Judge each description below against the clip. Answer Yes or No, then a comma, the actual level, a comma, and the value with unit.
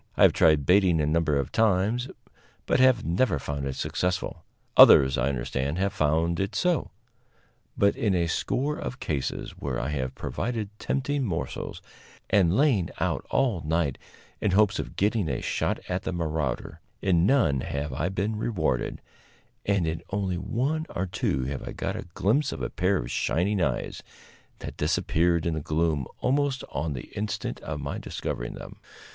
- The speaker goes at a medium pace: Yes, average, 170 wpm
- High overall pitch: No, very low, 90 Hz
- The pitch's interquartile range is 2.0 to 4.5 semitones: No, wide, 5.6 semitones